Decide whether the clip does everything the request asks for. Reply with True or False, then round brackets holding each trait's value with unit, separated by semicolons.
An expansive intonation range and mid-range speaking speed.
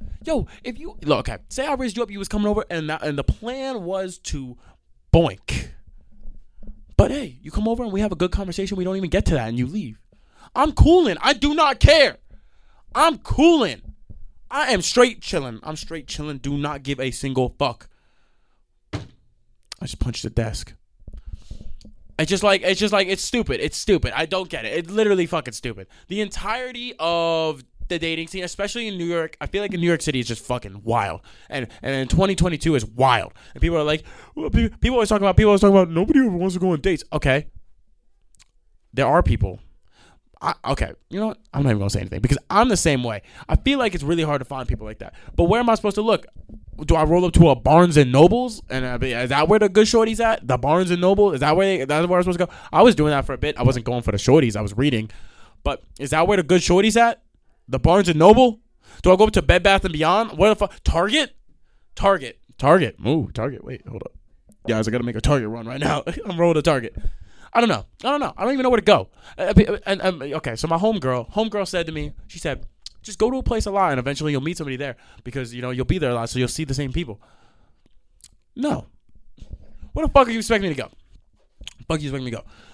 False (8.0 semitones; 245 wpm)